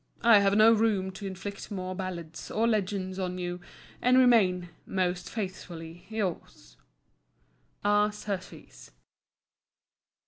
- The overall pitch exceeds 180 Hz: Yes, high, 190 Hz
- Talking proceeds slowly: Yes, slow, 110 wpm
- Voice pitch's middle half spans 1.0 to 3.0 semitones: Yes, narrow, 2.6 semitones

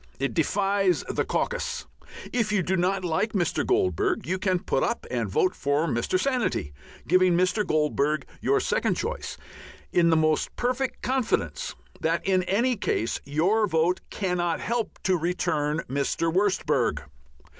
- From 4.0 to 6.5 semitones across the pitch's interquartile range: Yes, average, 4.9 semitones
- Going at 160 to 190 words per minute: No, average, 145 wpm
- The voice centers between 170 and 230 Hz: Yes, medium, 185 Hz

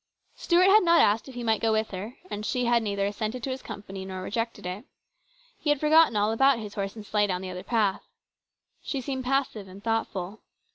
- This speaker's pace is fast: Yes, fast, 220 wpm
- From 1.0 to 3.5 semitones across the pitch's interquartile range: No, average, 4.4 semitones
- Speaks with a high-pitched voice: Yes, high, 220 Hz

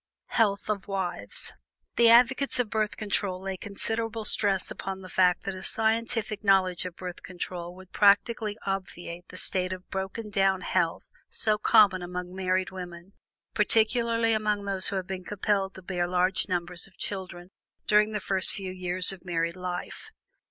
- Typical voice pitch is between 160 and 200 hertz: Yes, high, 190 Hz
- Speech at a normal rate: Yes, average, 165 wpm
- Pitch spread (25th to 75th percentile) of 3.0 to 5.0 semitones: No, narrow, 2.5 semitones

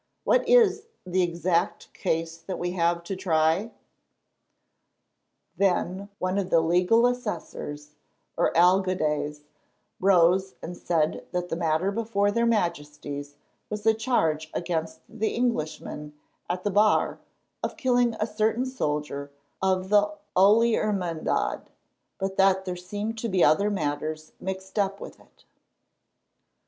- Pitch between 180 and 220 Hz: Yes, medium, 185 Hz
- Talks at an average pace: No, slow, 130 wpm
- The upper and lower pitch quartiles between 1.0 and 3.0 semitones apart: No, average, 4.1 semitones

